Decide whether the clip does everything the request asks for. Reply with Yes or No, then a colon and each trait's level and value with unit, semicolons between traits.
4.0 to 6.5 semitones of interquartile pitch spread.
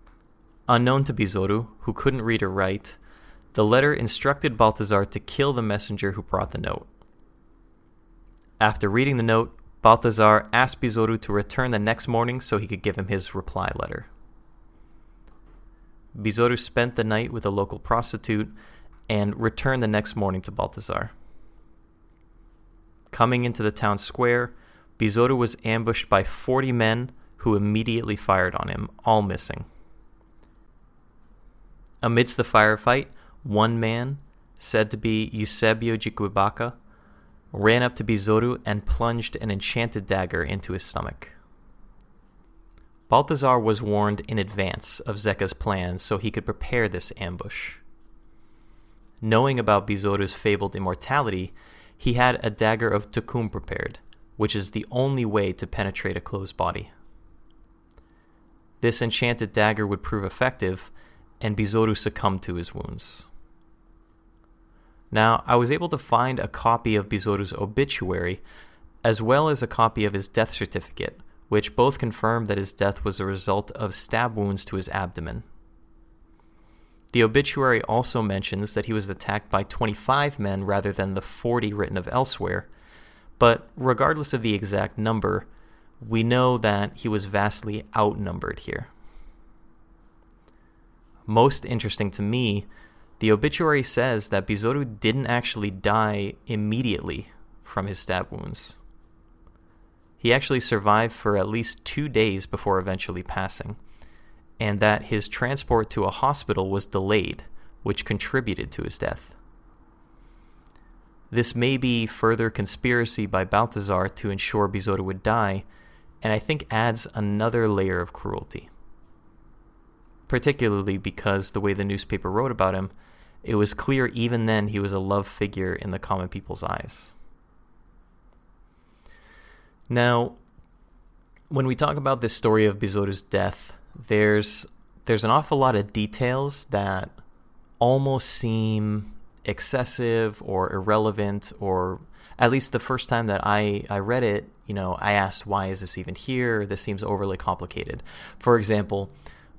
No: average, 3.3 semitones